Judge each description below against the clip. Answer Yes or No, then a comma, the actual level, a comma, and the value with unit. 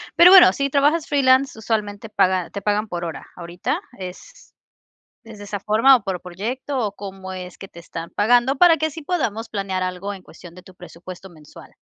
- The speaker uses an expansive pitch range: Yes, wide, 6.3 semitones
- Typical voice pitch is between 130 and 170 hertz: No, high, 205 Hz